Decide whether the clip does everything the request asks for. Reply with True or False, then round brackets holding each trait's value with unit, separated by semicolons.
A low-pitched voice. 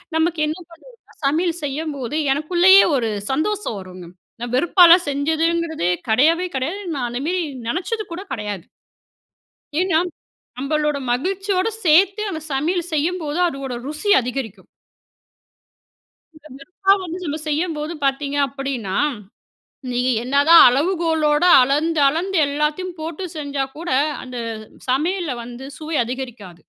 False (305 Hz)